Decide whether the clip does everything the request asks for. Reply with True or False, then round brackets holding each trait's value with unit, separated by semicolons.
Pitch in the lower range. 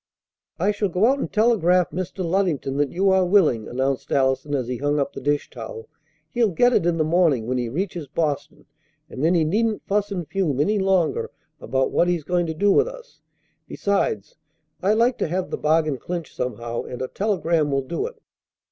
False (170 Hz)